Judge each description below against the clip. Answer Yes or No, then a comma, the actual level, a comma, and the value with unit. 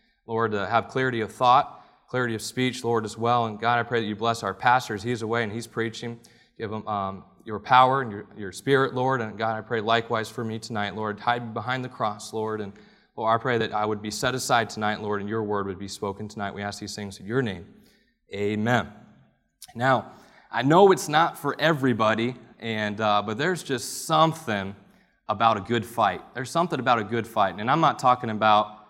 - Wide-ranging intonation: No, average, 2.9 semitones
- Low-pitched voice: Yes, low, 115 Hz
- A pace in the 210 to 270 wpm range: Yes, fast, 220 wpm